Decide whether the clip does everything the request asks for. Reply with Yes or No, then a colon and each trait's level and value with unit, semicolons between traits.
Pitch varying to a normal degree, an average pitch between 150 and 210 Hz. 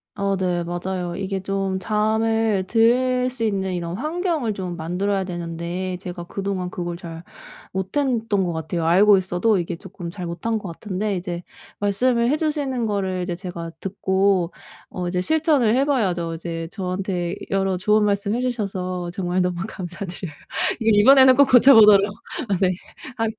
Yes: average, 3.9 semitones; high, 195 Hz